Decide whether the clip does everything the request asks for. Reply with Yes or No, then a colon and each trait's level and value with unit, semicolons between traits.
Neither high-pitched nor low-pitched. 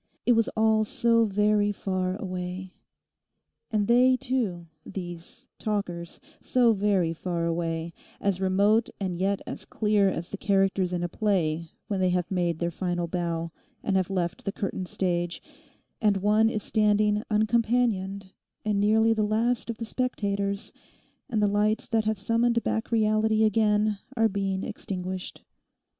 No: high, 200 Hz